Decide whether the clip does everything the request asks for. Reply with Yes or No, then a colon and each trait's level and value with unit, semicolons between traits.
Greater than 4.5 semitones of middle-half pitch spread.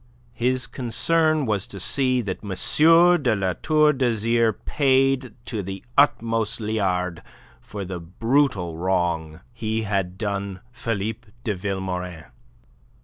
Yes: average, 4.9 semitones